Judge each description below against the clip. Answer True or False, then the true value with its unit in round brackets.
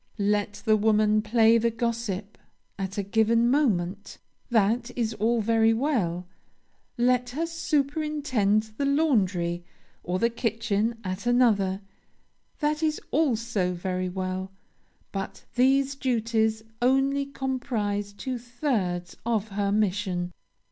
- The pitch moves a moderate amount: True (3.9 semitones)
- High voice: True (225 Hz)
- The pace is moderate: False (115 wpm)